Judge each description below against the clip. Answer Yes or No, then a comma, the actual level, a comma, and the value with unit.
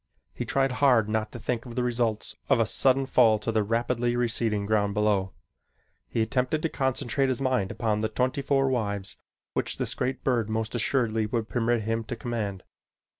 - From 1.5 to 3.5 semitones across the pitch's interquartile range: Yes, average, 2.7 semitones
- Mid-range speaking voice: No, low, 115 Hz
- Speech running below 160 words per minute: No, average, 185 wpm